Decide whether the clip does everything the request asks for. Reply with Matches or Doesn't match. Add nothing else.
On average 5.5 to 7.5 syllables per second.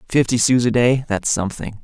Matches